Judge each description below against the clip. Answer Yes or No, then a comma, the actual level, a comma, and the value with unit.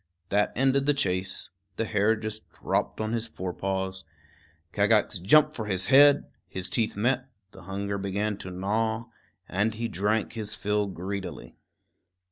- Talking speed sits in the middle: Yes, average, 150 wpm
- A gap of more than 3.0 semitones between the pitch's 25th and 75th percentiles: No, average, 2.7 semitones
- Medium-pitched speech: No, low, 105 Hz